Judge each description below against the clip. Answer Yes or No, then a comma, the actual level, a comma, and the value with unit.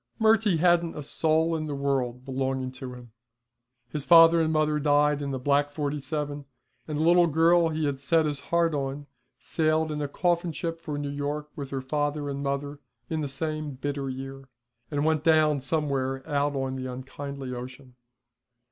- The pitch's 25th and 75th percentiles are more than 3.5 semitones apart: No, narrow, 2.5 semitones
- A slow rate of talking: No, average, 180 wpm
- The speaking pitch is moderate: Yes, medium, 145 Hz